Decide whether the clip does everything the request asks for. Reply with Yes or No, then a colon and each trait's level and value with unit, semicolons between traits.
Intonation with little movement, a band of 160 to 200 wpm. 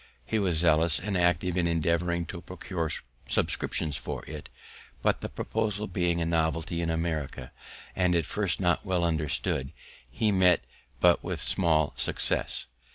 No: narrow, 2.1 semitones; average, 150 wpm